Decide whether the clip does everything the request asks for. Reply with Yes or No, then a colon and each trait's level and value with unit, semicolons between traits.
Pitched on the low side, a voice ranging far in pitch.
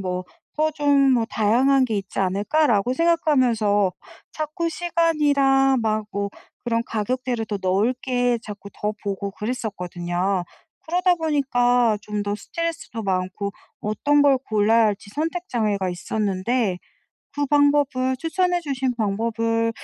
No: high, 235 Hz; wide, 5.7 semitones